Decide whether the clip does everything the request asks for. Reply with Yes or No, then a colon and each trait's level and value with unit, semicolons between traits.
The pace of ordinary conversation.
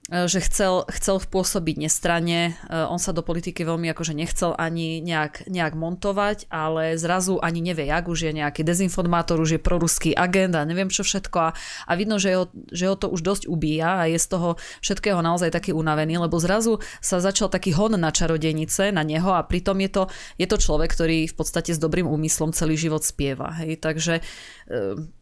No: fast, 190 wpm